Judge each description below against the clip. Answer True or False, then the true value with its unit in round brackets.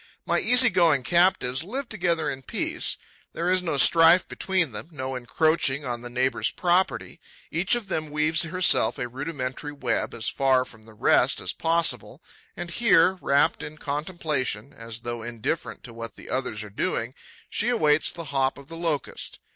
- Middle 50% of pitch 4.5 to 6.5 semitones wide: True (5.2 semitones)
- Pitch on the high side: False (150 Hz)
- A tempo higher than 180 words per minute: False (170 wpm)